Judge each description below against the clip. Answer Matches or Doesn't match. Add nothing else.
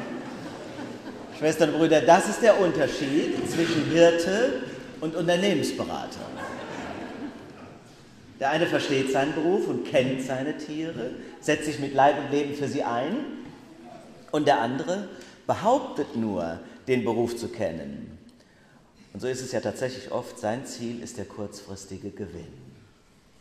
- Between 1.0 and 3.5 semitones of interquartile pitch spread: Doesn't match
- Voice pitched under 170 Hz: Matches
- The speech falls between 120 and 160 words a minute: Matches